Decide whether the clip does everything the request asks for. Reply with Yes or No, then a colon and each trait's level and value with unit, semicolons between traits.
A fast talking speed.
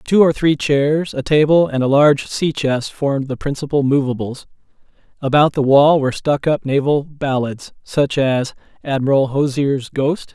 No: average, 160 wpm